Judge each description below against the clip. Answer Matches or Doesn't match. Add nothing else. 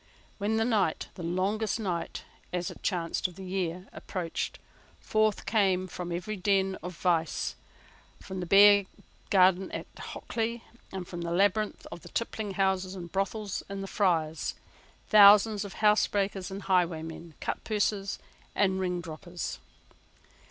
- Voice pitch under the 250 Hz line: Matches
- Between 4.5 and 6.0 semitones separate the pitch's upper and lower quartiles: Doesn't match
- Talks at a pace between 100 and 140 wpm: Matches